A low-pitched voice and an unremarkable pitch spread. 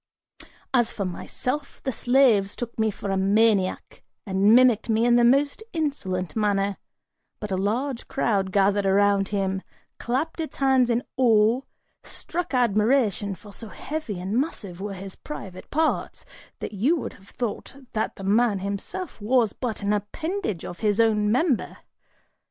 No: high, 215 Hz; average, 4.3 semitones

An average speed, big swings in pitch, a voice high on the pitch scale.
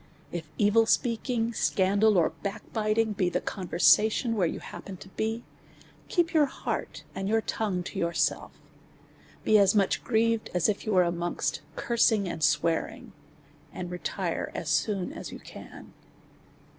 No: average, 150 wpm; average, 3.9 semitones; high, 205 Hz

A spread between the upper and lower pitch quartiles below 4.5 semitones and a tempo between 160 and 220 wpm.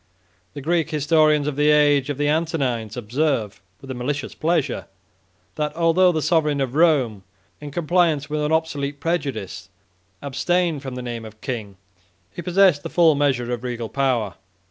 Yes: average, 4.1 semitones; average, 165 wpm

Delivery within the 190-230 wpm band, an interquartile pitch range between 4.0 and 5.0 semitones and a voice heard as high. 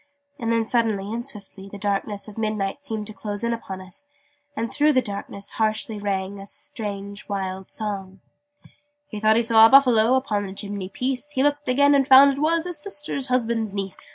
Yes: average, 195 wpm; average, 4.3 semitones; high, 220 Hz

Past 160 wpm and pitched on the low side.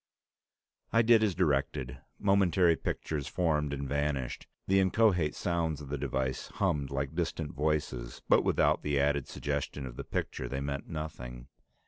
No: average, 150 wpm; very low, 75 Hz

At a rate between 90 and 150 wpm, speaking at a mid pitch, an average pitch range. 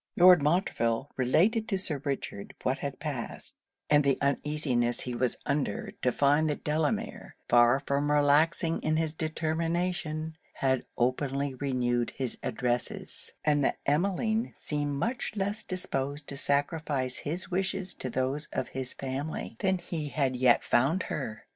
Yes: average, 145 wpm; medium, 145 Hz; average, 4.0 semitones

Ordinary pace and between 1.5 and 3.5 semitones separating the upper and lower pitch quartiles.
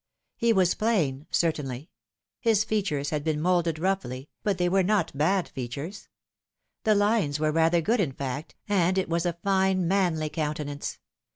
No: average, 160 wpm; average, 4.4 semitones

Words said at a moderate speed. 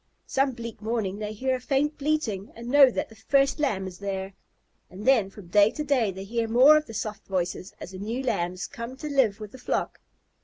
No: fast, 225 wpm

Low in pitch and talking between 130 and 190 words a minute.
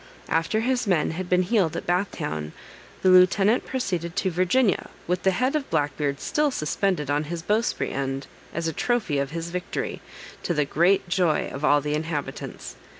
No: medium, 175 Hz; average, 185 wpm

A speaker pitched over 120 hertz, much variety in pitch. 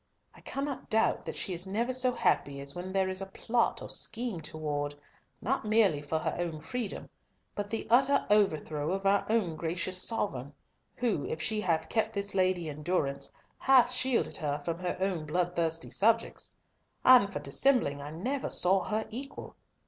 Yes: high, 190 Hz; wide, 5.9 semitones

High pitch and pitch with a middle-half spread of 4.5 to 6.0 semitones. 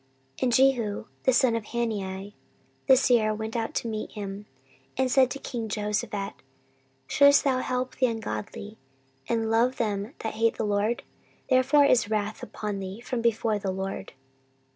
No: high, 225 Hz; average, 3.3 semitones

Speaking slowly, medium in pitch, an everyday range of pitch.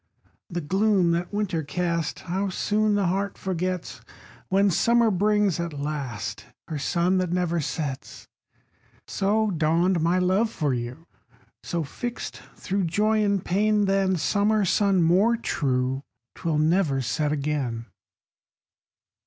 Yes: slow, 130 wpm; medium, 180 Hz; average, 4.6 semitones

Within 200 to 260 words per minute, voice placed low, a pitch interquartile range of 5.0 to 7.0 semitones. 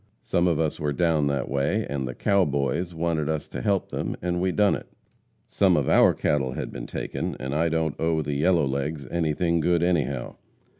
No: fast, 205 wpm; very low, 80 Hz; average, 3.5 semitones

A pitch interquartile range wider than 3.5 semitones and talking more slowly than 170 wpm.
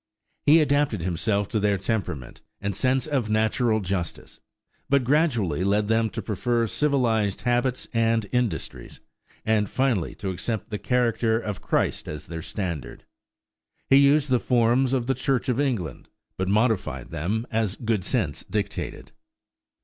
Yes: average, 4.1 semitones; average, 145 wpm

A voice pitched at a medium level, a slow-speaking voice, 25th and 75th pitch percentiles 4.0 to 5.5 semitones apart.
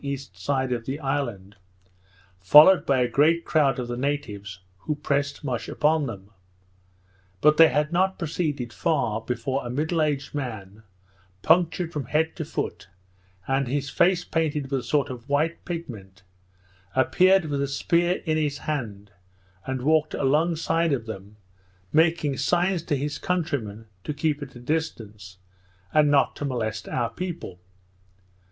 No: medium, 145 Hz; average, 155 wpm; average, 4.6 semitones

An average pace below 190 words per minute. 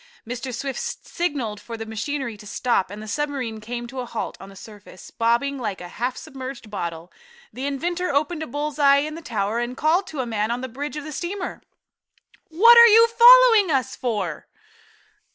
No: average, 200 wpm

